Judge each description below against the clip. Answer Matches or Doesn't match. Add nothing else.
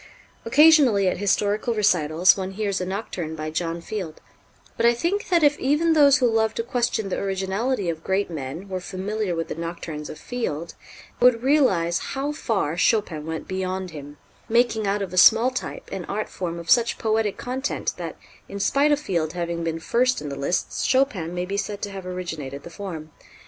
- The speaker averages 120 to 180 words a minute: Doesn't match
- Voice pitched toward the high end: Matches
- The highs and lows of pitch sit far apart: Matches